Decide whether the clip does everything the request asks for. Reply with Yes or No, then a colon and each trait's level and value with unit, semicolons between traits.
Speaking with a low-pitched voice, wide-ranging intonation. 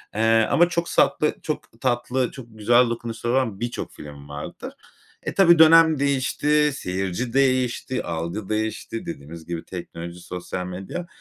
Yes: low, 115 Hz; wide, 6.7 semitones